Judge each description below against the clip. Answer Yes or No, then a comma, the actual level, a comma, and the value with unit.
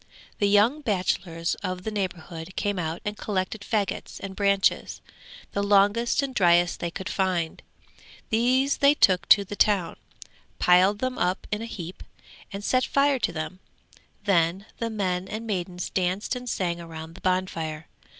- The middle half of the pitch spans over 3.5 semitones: No, average, 3.1 semitones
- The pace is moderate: Yes, average, 160 wpm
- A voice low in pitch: No, high, 195 Hz